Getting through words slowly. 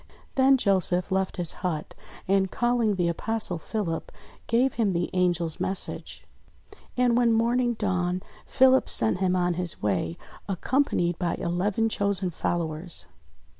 Yes: slow, 130 wpm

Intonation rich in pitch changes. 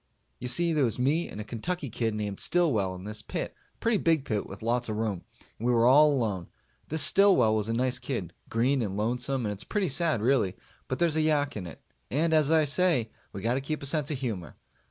Yes: wide, 6.0 semitones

